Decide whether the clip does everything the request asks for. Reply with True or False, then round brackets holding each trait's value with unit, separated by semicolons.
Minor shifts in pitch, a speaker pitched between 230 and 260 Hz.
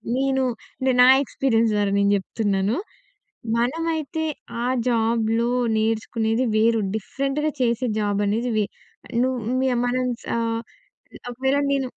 False (3.3 semitones; 235 Hz)